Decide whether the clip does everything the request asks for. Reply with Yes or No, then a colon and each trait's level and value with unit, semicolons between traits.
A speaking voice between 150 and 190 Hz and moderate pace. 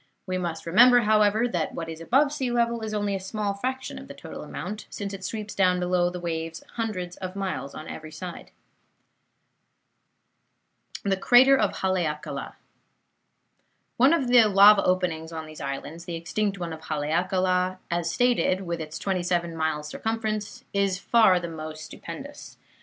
Yes: medium, 185 Hz; average, 160 wpm